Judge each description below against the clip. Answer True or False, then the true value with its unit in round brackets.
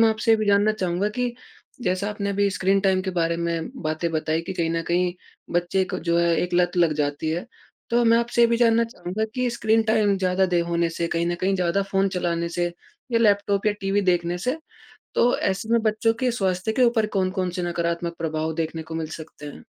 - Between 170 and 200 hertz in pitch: True (185 Hz)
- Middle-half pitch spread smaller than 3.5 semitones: False (3.8 semitones)